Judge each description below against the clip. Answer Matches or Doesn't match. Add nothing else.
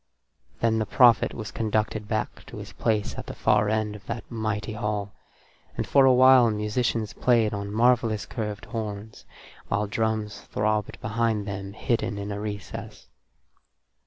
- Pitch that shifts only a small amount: Matches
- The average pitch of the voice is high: Doesn't match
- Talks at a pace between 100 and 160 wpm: Matches